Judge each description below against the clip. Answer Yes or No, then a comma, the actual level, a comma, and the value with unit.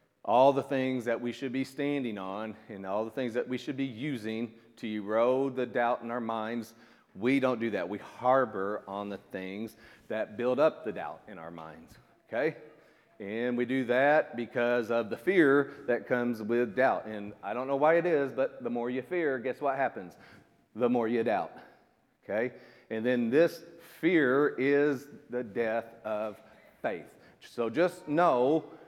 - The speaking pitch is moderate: No, low, 120 Hz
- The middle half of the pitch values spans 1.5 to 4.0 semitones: Yes, average, 3.2 semitones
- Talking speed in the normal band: Yes, average, 180 wpm